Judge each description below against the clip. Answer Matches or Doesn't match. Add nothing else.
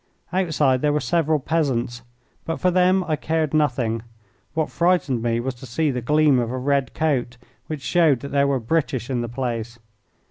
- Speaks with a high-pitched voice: Doesn't match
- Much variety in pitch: Doesn't match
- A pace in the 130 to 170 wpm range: Doesn't match